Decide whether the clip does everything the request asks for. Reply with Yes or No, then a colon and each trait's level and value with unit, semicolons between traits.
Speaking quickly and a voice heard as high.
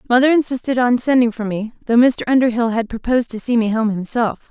Yes: fast, 215 wpm; high, 235 Hz